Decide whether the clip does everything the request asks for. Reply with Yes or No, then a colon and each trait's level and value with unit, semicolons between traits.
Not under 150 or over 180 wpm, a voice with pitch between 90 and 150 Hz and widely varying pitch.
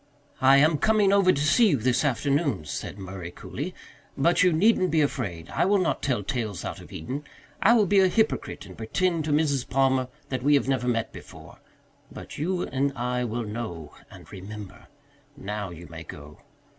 No: average, 190 wpm; low, 135 Hz; wide, 7.1 semitones